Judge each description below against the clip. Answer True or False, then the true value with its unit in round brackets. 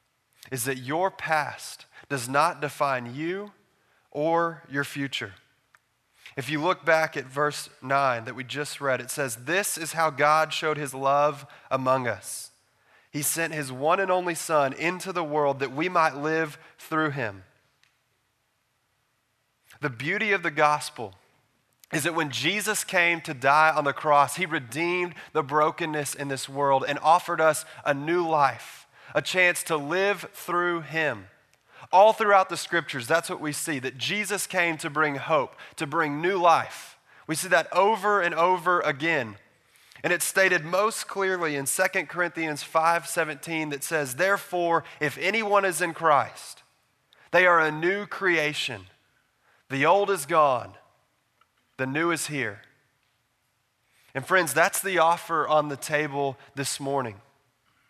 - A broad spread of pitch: False (3.8 semitones)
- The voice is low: False (150 Hz)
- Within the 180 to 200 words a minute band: False (155 wpm)